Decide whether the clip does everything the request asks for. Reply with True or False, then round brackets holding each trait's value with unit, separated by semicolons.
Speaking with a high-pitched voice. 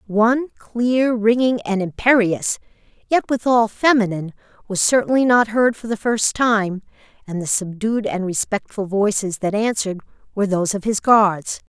True (215 Hz)